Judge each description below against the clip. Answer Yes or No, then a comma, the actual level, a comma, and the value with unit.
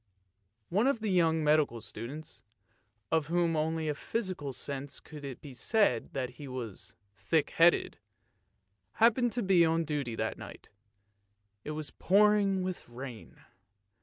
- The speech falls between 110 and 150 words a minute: Yes, average, 145 wpm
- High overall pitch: No, medium, 155 Hz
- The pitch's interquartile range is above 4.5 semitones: Yes, average, 5.2 semitones